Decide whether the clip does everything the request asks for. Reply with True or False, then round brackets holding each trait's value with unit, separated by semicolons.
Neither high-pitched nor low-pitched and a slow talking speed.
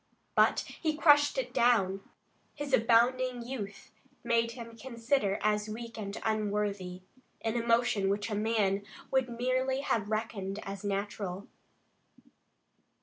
False (225 Hz; 120 wpm)